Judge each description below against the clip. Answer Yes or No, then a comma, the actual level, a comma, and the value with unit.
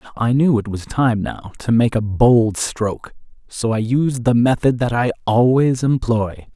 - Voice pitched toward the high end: No, low, 120 Hz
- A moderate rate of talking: Yes, average, 185 wpm